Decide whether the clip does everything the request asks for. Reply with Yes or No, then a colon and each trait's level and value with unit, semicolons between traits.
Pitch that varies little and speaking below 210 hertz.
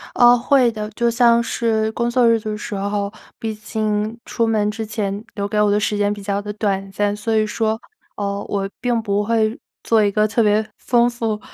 No: narrow, 1.9 semitones; high, 215 Hz